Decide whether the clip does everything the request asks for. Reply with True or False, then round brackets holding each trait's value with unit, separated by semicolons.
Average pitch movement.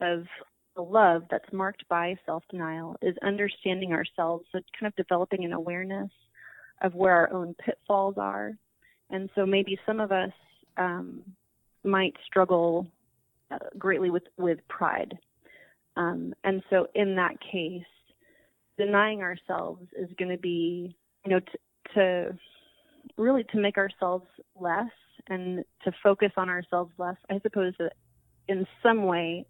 False (2.2 semitones)